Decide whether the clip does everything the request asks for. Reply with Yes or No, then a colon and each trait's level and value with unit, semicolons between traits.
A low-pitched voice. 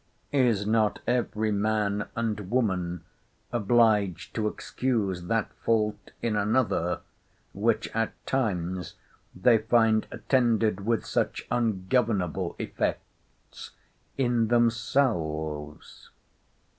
Yes: low, 110 Hz